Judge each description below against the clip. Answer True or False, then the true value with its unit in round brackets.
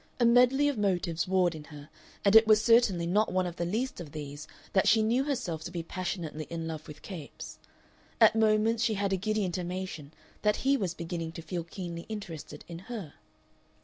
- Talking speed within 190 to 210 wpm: True (200 wpm)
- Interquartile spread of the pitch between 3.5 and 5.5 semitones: True (4.6 semitones)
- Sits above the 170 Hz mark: True (185 Hz)